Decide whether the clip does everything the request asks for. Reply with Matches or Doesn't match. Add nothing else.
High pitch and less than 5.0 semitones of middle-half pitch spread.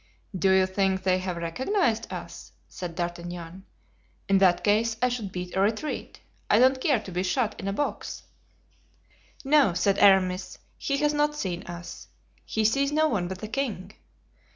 Doesn't match